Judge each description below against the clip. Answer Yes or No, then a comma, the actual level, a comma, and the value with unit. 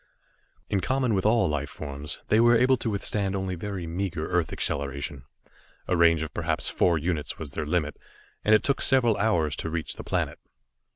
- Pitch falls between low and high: No, very low, 90 Hz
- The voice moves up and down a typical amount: No, wide, 5.7 semitones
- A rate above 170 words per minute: Yes, average, 185 wpm